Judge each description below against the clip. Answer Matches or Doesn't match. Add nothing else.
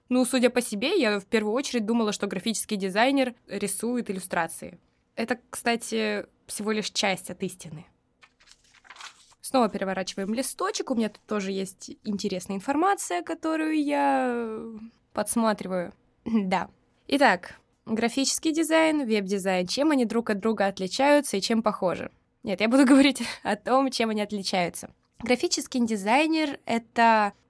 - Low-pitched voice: Doesn't match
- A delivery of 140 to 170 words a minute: Doesn't match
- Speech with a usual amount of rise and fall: Matches